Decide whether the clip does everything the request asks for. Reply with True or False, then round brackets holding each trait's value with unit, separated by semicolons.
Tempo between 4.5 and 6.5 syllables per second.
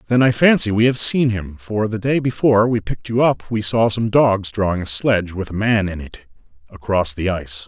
True (5.4 syllables/s)